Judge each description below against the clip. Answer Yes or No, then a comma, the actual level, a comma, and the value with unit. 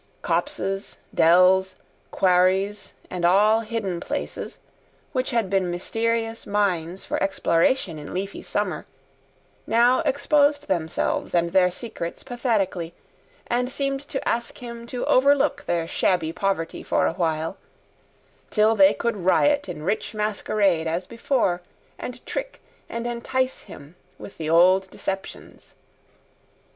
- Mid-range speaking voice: No, high, 195 Hz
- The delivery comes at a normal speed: No, slow, 125 wpm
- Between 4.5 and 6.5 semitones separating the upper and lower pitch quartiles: Yes, average, 4.9 semitones